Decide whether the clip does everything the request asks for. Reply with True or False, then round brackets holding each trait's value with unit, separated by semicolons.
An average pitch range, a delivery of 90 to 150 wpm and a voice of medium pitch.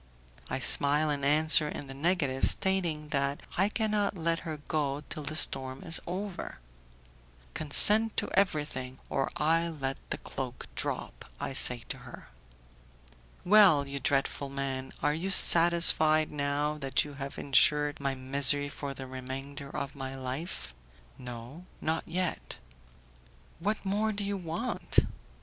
True (3.7 semitones; 140 wpm; 150 Hz)